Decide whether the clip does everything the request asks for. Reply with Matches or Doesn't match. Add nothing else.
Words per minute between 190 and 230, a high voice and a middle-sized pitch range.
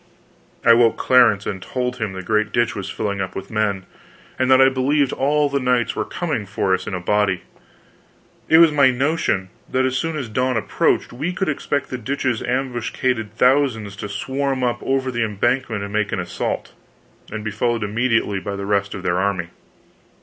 Doesn't match